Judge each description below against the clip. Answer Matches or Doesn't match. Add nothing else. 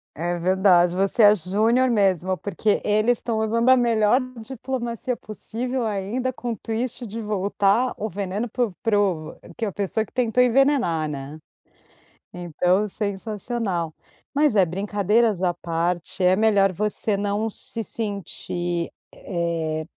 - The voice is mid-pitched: Doesn't match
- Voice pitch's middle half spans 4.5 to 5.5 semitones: Doesn't match